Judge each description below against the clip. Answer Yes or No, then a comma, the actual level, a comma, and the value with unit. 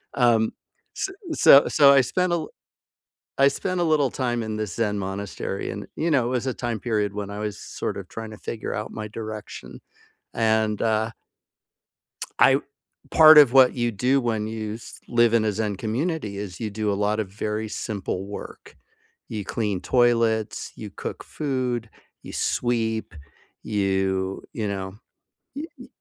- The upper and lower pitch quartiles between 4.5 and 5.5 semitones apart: No, average, 3.0 semitones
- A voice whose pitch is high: No, low, 110 Hz